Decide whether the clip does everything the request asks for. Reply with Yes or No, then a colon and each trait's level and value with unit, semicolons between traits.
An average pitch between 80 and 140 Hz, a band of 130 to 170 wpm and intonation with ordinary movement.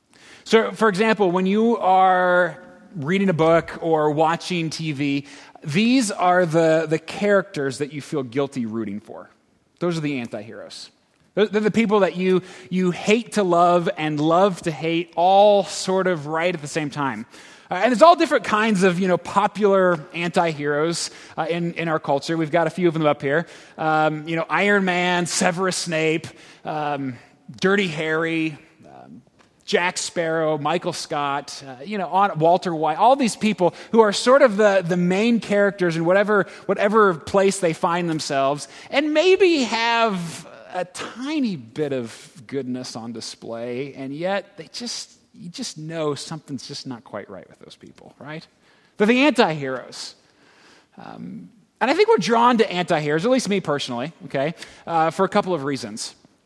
No: medium, 175 Hz; average, 165 wpm; average, 4.5 semitones